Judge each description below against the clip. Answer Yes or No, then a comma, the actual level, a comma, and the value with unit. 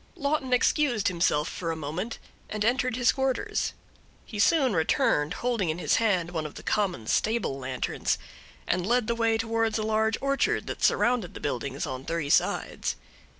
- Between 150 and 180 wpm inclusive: Yes, average, 170 wpm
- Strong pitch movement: Yes, wide, 6.7 semitones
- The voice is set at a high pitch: Yes, high, 215 Hz